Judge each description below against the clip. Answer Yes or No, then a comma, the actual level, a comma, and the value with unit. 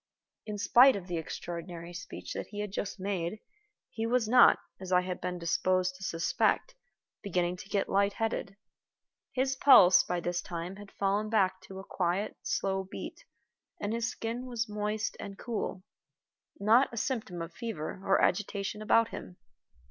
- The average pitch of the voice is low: No, high, 195 Hz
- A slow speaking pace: No, average, 165 wpm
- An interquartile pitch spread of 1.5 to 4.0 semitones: Yes, average, 3.4 semitones